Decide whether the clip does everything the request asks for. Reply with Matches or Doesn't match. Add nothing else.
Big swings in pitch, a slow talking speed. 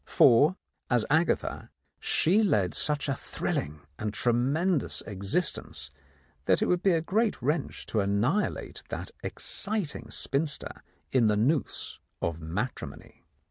Matches